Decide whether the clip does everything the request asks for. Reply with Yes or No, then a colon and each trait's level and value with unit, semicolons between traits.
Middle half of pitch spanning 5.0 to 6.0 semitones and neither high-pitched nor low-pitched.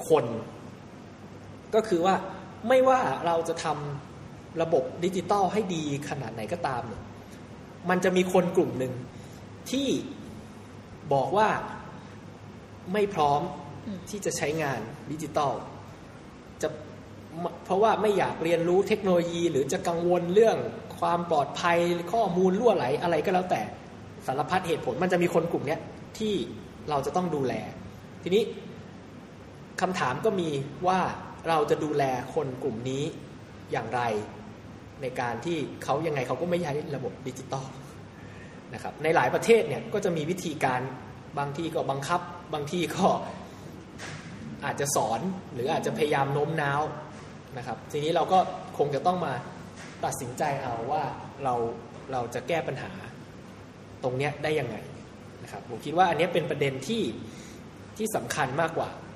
Yes: wide, 5.4 semitones; medium, 155 Hz